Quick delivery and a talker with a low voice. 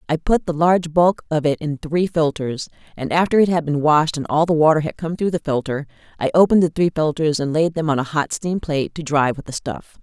No: fast, 255 wpm; medium, 155 Hz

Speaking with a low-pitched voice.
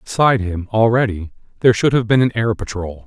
Yes: low, 110 Hz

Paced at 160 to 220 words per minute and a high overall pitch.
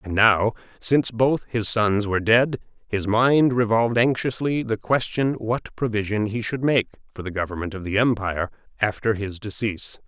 No: average, 165 wpm; low, 110 Hz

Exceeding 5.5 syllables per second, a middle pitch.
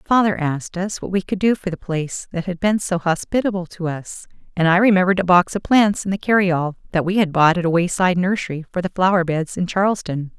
Yes: 6.0 syllables/s; medium, 180 Hz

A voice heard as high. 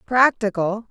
Yes: high, 220 Hz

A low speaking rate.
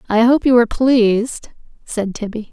No: average, 165 wpm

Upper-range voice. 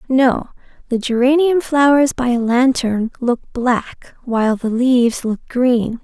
Yes: very high, 250 Hz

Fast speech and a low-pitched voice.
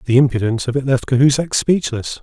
No: average, 190 wpm; low, 130 Hz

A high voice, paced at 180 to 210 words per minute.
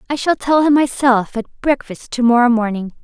Yes: very high, 250 Hz; average, 200 wpm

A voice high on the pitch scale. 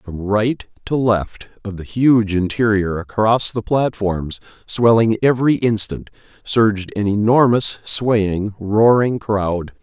No: low, 110 Hz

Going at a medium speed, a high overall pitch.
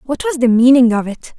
No: fast, 260 wpm; high, 240 Hz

